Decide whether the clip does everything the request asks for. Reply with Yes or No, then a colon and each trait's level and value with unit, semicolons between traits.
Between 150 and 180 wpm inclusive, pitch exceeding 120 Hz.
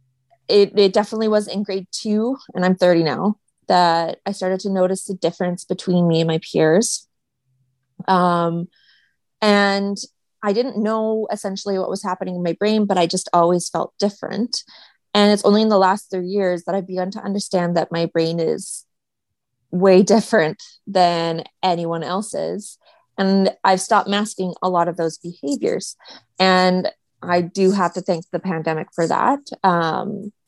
Yes: average, 165 wpm; medium, 185 Hz